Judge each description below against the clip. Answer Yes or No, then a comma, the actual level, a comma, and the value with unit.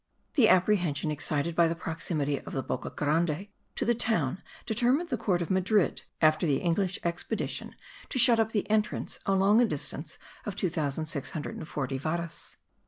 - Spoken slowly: No, average, 155 wpm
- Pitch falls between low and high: Yes, medium, 170 Hz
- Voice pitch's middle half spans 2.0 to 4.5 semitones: No, wide, 5.4 semitones